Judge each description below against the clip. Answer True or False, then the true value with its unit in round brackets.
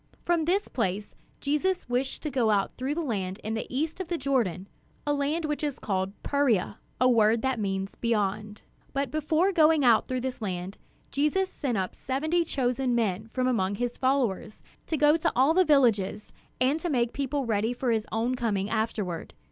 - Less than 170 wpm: False (190 wpm)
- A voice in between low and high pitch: False (250 Hz)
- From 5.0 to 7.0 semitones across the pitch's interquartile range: True (5.4 semitones)